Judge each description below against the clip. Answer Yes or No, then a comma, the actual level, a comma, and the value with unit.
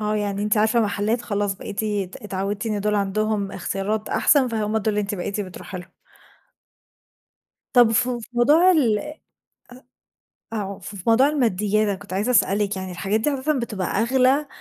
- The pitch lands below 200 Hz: No, high, 210 Hz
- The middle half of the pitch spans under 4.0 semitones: Yes, average, 2.9 semitones